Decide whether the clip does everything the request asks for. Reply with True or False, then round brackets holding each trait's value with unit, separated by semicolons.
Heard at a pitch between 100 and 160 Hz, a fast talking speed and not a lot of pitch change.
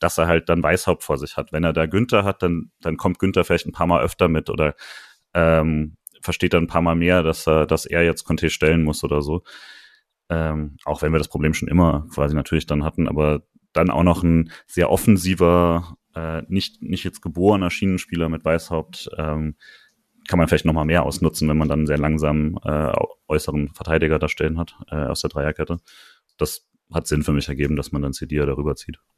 False (80 Hz; 210 wpm; 1.9 semitones)